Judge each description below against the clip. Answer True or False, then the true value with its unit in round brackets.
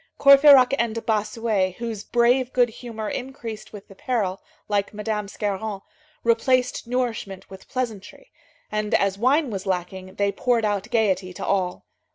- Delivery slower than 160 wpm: True (145 wpm)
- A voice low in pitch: False (220 Hz)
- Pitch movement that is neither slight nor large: True (3.5 semitones)